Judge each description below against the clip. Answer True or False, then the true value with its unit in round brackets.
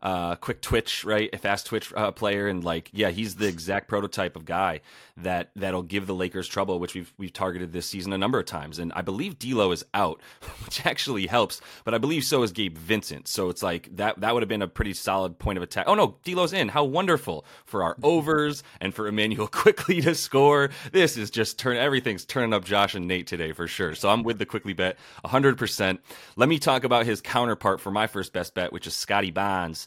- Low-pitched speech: True (100 Hz)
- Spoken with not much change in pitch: False (3.8 semitones)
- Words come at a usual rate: False (240 wpm)